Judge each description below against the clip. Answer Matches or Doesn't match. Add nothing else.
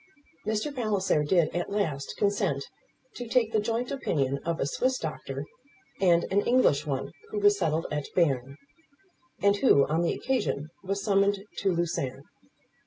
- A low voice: Doesn't match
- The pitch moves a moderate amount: Doesn't match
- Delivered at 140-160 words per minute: Matches